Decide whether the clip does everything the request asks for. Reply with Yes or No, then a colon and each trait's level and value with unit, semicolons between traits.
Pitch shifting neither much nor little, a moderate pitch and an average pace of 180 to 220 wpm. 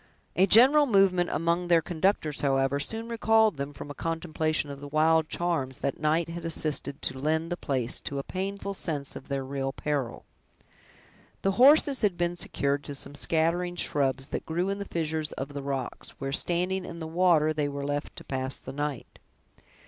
Yes: average, 4.0 semitones; medium, 160 Hz; average, 185 wpm